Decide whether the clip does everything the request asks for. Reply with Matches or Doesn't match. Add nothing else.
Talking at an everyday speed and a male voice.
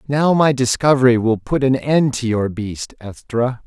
Matches